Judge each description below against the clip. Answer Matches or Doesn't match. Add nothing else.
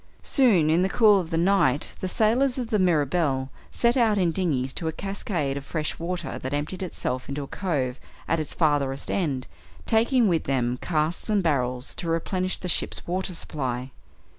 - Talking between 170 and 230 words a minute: Matches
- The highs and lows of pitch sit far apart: Matches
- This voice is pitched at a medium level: Matches